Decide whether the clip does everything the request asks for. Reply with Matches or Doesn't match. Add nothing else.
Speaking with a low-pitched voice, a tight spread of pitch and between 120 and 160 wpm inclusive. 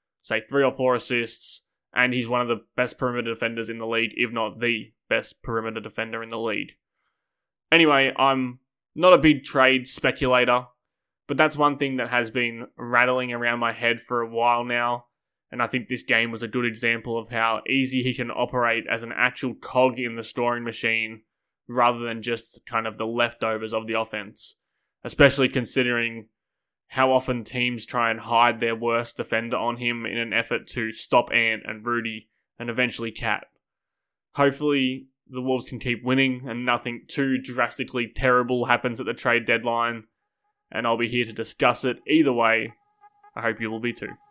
Doesn't match